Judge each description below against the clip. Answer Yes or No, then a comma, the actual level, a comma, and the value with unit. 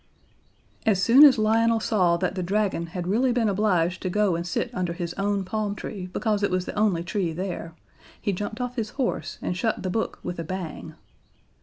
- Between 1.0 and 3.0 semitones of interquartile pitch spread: No, average, 3.4 semitones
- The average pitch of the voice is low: No, high, 195 Hz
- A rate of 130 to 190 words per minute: No, fast, 205 wpm